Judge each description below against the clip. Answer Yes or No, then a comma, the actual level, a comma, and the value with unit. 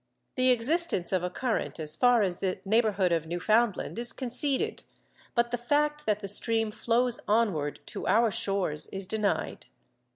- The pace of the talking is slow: No, average, 160 wpm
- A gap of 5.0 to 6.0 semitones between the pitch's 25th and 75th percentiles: No, average, 4.1 semitones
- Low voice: No, high, 220 Hz